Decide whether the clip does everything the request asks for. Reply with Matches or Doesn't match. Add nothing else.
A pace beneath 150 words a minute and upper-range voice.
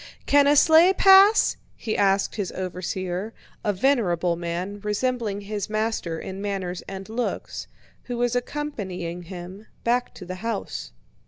Matches